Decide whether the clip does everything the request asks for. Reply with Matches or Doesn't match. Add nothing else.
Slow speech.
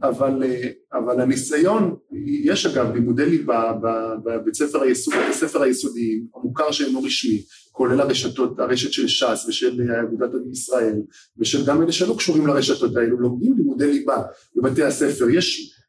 Doesn't match